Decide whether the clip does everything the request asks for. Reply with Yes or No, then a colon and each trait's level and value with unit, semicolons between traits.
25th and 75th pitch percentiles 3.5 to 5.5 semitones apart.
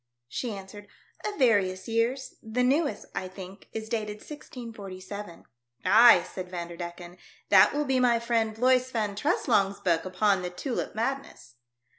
Yes: average, 4.7 semitones